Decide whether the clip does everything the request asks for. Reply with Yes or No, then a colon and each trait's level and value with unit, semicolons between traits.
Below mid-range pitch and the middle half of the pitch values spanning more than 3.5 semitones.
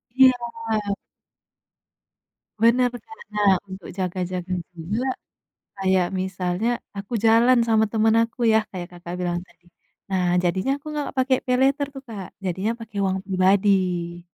No: high, 195 Hz; average, 4.1 semitones